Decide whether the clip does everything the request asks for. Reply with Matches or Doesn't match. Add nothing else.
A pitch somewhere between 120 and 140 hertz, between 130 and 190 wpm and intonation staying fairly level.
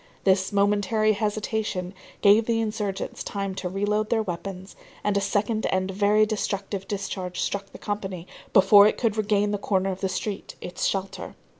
Doesn't match